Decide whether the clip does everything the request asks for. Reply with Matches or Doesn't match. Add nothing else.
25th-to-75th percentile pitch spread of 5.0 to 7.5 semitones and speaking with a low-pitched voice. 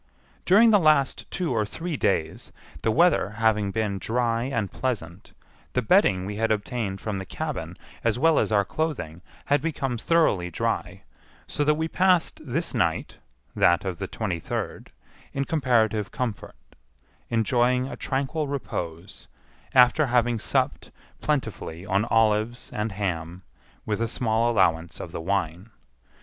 Matches